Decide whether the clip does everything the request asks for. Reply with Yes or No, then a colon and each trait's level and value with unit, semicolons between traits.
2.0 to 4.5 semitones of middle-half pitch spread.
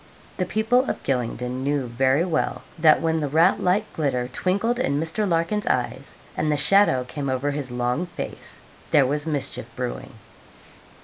No: wide, 5.6 semitones